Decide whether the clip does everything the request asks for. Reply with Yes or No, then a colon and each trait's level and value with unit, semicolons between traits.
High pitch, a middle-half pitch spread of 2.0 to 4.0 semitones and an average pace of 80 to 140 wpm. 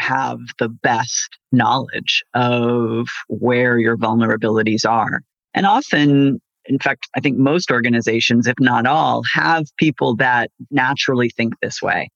No: low, 120 Hz; average, 2.9 semitones; slow, 135 wpm